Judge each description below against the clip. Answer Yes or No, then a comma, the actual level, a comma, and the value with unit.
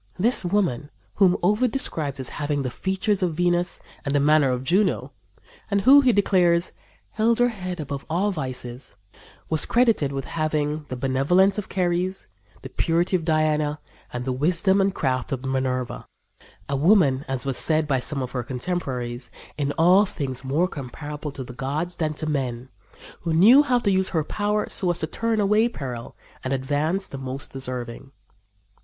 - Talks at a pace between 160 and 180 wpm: Yes, average, 175 wpm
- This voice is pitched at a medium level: Yes, medium, 155 Hz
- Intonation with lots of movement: Yes, wide, 5.9 semitones